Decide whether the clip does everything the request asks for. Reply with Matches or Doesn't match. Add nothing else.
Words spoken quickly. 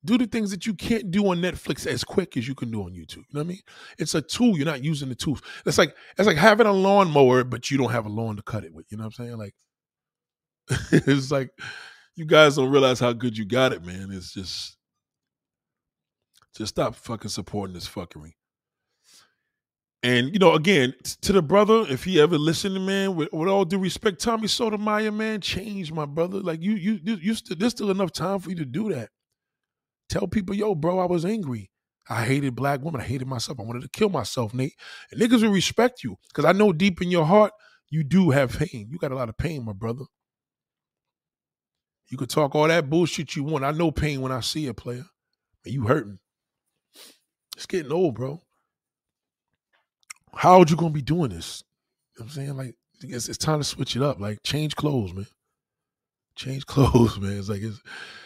Matches